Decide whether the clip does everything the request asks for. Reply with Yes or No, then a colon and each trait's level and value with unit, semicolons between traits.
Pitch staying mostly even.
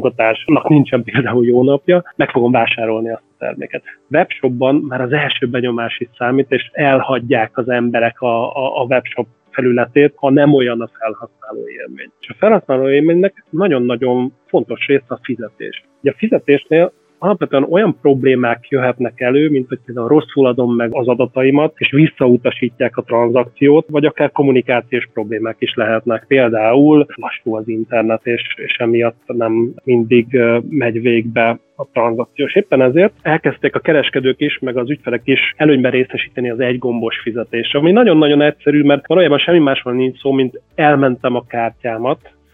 No: average, 3.5 semitones